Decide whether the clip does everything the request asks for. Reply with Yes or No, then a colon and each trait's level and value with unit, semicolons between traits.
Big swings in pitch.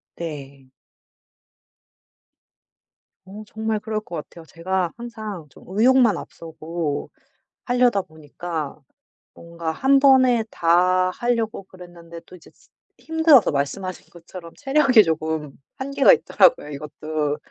Yes: wide, 6.3 semitones